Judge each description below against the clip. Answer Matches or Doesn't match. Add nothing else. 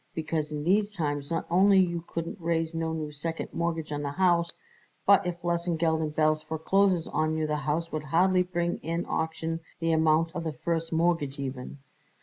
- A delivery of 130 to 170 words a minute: Doesn't match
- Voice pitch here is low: Doesn't match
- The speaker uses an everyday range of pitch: Doesn't match